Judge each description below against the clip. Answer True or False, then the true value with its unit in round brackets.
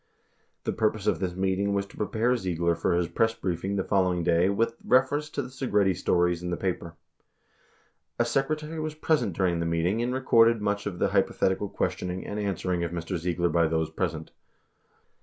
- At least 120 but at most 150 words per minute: False (185 wpm)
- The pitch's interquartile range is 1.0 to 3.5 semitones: False (4.6 semitones)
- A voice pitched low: True (95 Hz)